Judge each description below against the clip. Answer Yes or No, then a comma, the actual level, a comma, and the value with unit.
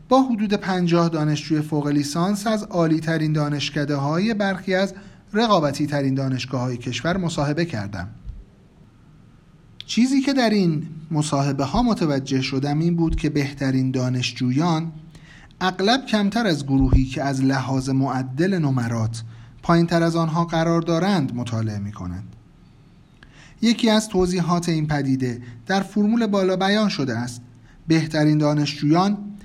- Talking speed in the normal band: Yes, average, 130 wpm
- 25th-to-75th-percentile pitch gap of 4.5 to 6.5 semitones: Yes, wide, 5.6 semitones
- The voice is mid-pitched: Yes, medium, 155 Hz